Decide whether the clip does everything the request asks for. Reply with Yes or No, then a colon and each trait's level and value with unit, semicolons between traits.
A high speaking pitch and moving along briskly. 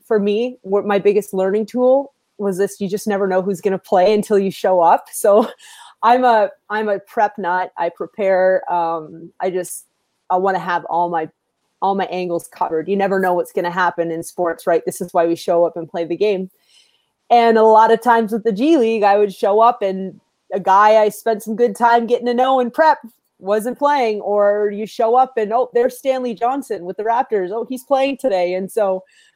Yes: high, 205 Hz; fast, 225 wpm